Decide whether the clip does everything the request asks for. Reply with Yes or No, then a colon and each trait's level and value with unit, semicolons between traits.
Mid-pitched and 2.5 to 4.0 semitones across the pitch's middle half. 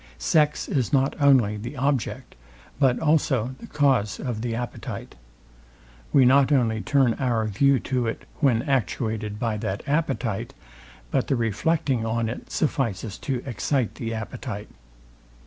No: low, 125 Hz; average, 3.7 semitones